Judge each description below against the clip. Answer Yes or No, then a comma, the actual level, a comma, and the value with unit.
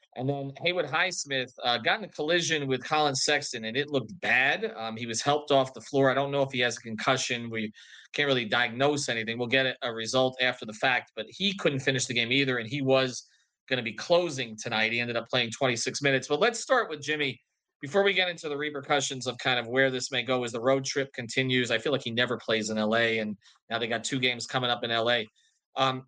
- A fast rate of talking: Yes, fast, 245 wpm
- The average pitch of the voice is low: Yes, low, 130 Hz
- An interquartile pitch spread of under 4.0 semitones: Yes, average, 2.8 semitones